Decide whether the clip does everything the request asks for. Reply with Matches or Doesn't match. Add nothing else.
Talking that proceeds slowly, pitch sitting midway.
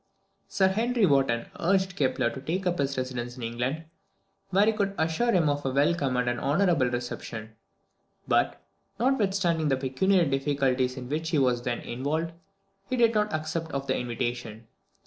Doesn't match